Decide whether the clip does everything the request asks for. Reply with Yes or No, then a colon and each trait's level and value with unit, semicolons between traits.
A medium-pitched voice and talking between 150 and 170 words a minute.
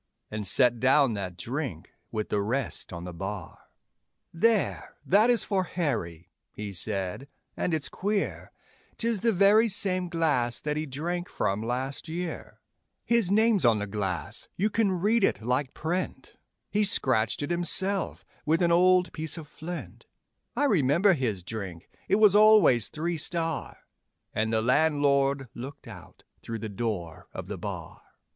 Yes: medium, 145 Hz; average, 155 wpm